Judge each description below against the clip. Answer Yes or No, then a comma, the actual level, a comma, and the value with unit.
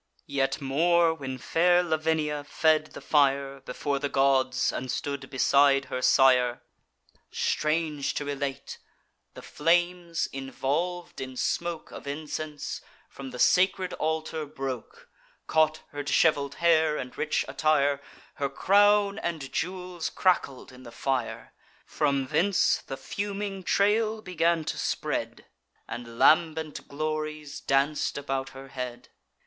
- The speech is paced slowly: Yes, slow, 125 wpm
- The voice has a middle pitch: Yes, medium, 150 Hz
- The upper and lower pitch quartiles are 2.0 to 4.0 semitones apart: Yes, average, 3.6 semitones